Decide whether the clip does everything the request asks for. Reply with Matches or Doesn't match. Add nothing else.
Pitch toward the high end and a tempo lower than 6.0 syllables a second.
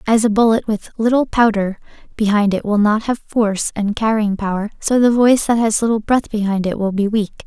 Matches